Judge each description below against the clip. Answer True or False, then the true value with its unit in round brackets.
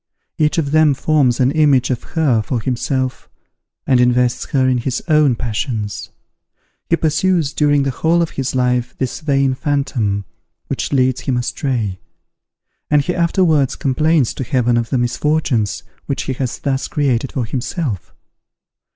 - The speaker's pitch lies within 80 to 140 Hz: True (135 Hz)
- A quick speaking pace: False (150 wpm)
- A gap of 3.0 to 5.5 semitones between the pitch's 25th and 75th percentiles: True (3.4 semitones)